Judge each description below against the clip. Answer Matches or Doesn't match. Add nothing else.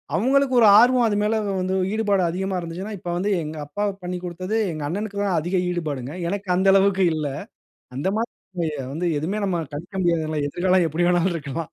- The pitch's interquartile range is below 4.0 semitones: Matches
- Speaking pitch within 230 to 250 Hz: Doesn't match